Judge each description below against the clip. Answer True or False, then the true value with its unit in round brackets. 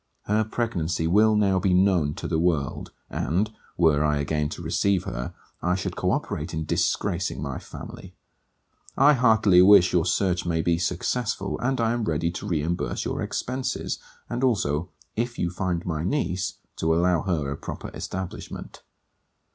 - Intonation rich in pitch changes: False (4.5 semitones)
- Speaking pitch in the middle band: False (90 Hz)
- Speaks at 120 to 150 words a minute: False (165 wpm)